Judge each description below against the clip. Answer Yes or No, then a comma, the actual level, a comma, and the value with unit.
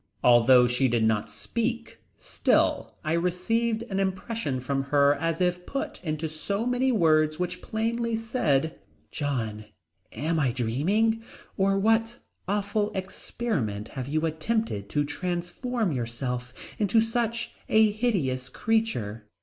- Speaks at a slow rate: Yes, slow, 125 wpm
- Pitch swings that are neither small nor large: No, wide, 8.9 semitones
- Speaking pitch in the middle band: Yes, medium, 175 Hz